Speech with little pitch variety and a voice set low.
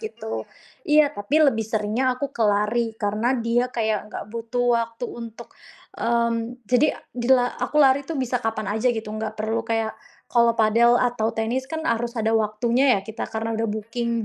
No: narrow, 2.0 semitones; high, 230 Hz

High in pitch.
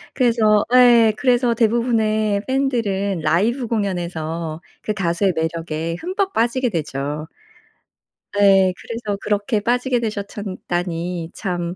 Yes: high, 205 Hz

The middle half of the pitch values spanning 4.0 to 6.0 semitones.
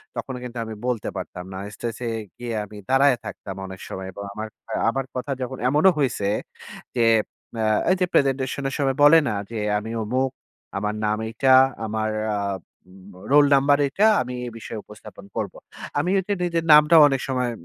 Yes: average, 4.4 semitones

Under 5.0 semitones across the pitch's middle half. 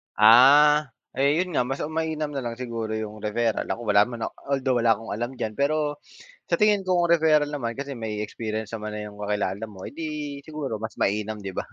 No: wide, 5.5 semitones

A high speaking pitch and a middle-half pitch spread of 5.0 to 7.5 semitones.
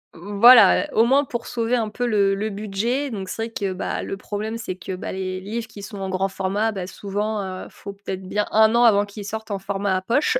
No: high, 205 Hz; narrow, 2.5 semitones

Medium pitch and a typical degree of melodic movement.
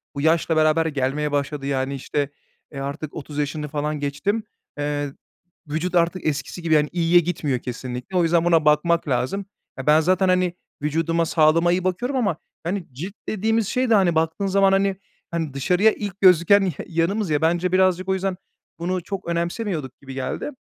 Yes: medium, 165 Hz; average, 3.9 semitones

